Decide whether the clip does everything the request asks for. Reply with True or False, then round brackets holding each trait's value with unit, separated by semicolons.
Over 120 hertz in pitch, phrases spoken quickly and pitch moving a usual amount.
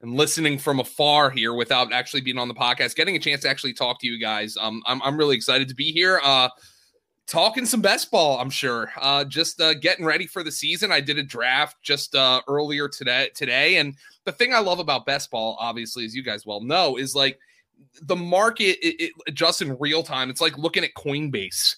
True (140 Hz; 225 wpm; 4.3 semitones)